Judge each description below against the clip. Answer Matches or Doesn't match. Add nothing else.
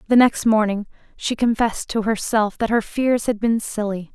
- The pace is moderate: Matches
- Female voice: Matches